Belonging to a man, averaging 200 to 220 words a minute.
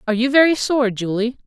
No: female; fast, 205 wpm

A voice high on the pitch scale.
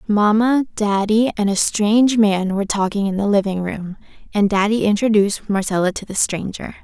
Yes: high, 205 Hz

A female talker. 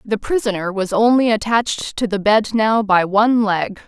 Yes: female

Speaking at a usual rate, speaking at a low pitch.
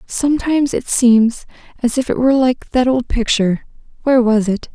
No: average, 165 wpm; high, 245 Hz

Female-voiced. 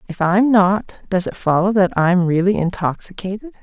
Yes: female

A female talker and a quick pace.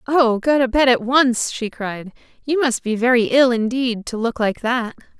Yes: female; fast, 210 wpm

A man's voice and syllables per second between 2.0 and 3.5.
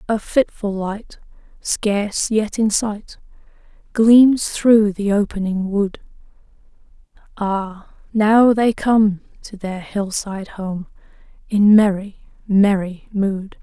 No: female; 3.1 syllables/s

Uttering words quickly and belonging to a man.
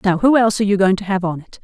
No: fast, 365 wpm; female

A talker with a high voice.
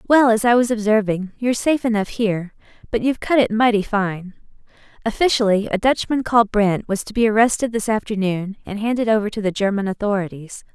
Yes: high, 215 Hz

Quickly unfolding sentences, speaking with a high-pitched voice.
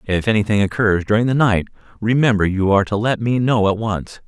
No: fast, 210 wpm; low, 105 Hz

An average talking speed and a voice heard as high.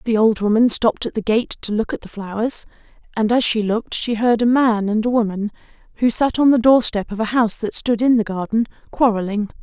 No: fast, 235 wpm; high, 225 Hz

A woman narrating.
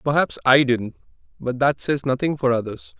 No: male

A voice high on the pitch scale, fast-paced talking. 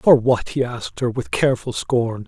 No: low, 120 Hz; fast, 210 wpm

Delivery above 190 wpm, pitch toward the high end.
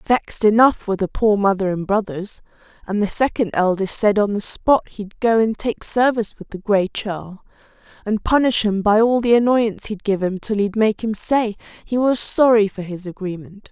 Yes: average, 200 wpm; high, 210 Hz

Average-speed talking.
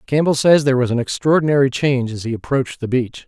No: fast, 220 wpm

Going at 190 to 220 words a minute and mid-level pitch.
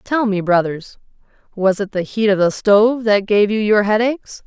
No: average, 200 wpm; high, 210 Hz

